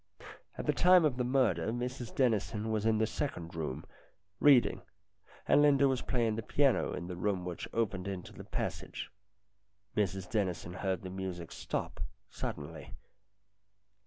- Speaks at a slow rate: No, average, 150 wpm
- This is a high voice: No, low, 105 Hz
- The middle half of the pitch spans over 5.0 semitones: Yes, wide, 5.4 semitones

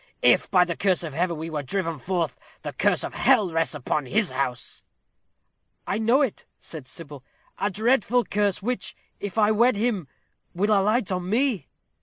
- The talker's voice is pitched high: Yes, high, 195 Hz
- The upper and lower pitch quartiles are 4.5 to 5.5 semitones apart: Yes, average, 4.8 semitones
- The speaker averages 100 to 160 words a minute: No, average, 175 wpm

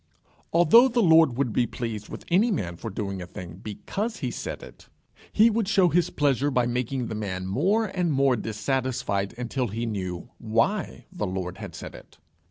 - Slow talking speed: No, average, 185 wpm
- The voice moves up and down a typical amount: No, wide, 8.9 semitones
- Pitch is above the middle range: No, low, 125 Hz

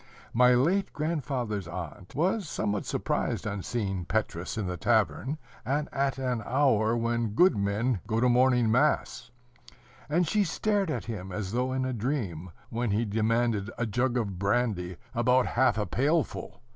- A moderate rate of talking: Yes, average, 160 wpm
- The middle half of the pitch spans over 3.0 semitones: Yes, average, 4.2 semitones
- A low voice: Yes, low, 120 Hz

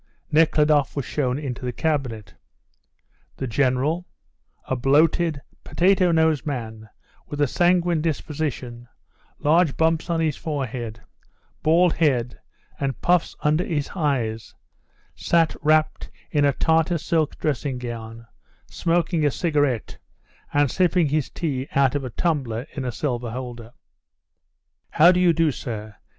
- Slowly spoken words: Yes, slow, 130 wpm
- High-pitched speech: No, medium, 145 Hz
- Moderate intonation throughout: Yes, average, 4.4 semitones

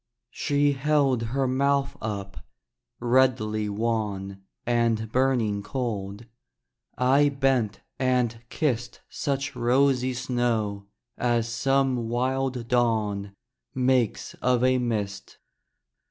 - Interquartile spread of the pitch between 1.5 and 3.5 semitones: Yes, average, 3.2 semitones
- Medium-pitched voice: No, low, 120 Hz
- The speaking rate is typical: No, slow, 95 wpm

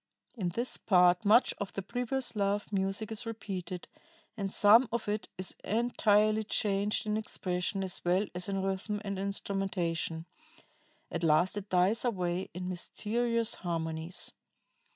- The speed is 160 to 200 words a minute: No, average, 140 wpm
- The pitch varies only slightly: No, average, 3.0 semitones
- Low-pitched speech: No, high, 195 Hz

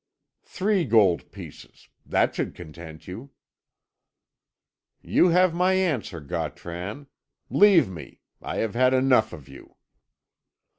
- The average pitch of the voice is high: No, low, 120 Hz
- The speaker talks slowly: Yes, slow, 110 wpm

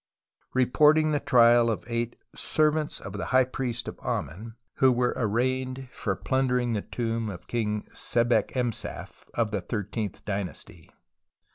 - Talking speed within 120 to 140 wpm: Yes, slow, 135 wpm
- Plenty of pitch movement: No, average, 3.2 semitones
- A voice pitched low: Yes, low, 120 Hz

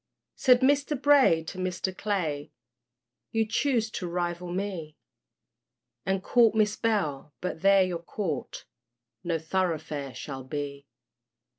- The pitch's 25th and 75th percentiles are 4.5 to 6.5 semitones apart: Yes, average, 5.2 semitones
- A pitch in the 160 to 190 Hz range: Yes, medium, 185 Hz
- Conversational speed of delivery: No, slow, 120 wpm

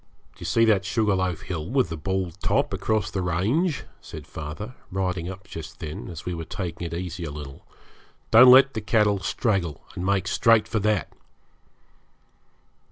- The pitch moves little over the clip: No, average, 4.1 semitones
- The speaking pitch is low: Yes, very low, 95 Hz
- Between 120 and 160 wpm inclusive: No, average, 175 wpm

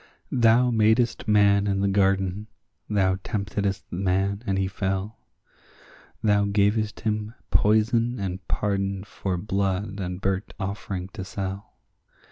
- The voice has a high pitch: No, low, 100 Hz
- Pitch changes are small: Yes, narrow, 1.7 semitones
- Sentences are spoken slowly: Yes, slow, 120 wpm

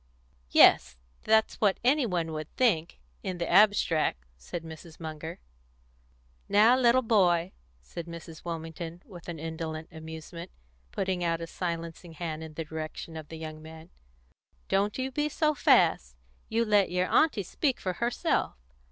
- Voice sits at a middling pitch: Yes, medium, 170 Hz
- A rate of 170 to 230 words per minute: No, average, 145 wpm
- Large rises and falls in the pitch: No, average, 4.3 semitones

